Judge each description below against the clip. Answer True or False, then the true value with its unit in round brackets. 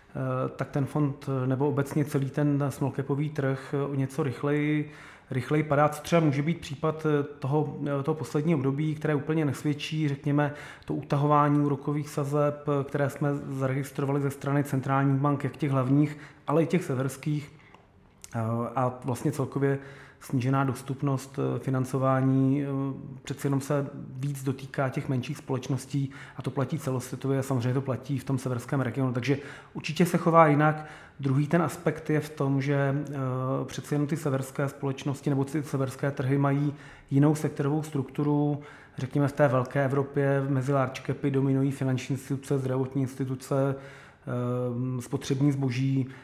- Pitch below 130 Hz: False (140 Hz)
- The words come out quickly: False (145 wpm)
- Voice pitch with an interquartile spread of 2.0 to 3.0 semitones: False (1.6 semitones)